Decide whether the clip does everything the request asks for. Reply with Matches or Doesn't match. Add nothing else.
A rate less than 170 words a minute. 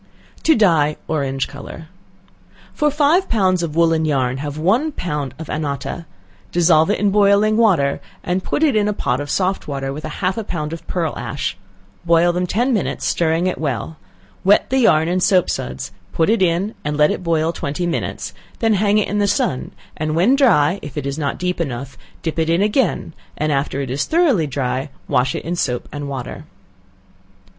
Doesn't match